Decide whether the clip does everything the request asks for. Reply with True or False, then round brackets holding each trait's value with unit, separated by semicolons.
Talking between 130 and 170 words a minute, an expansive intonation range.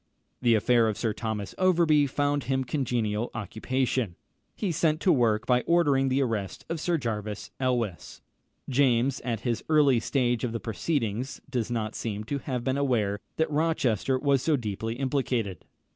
False (160 wpm; 4.0 semitones)